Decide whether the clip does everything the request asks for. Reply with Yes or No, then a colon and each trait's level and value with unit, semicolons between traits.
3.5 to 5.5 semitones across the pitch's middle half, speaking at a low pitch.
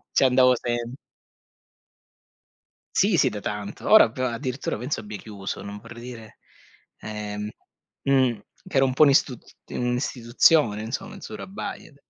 Yes: average, 3.9 semitones; low, 120 Hz